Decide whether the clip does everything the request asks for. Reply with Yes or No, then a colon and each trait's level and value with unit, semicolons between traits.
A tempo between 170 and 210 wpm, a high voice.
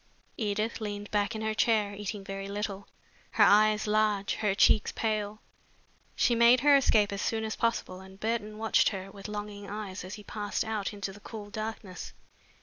Yes: average, 180 wpm; high, 210 Hz